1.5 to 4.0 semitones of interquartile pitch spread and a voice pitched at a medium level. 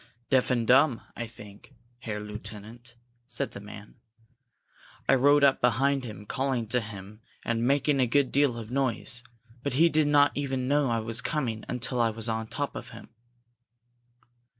No: average, 3.6 semitones; low, 125 Hz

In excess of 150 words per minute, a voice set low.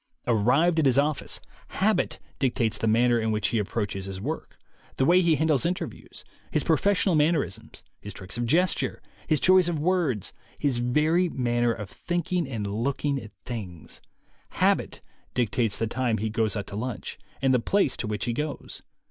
Yes: average, 180 wpm; low, 125 Hz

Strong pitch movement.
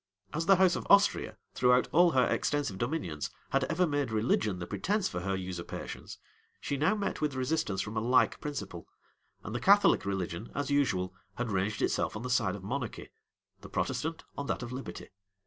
Yes: wide, 7.2 semitones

